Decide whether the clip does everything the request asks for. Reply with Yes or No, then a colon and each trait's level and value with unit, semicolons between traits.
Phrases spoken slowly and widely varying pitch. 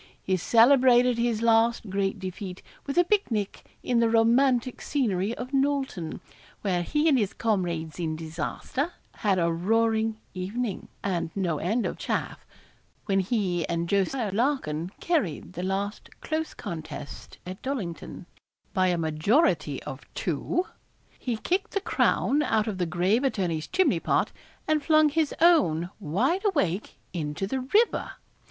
No: average, 145 wpm; wide, 6.9 semitones